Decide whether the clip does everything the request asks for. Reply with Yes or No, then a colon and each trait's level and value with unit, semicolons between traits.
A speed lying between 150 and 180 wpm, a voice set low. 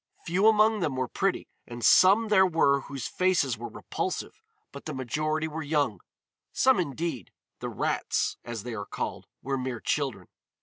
No: average, 165 wpm; medium, 145 Hz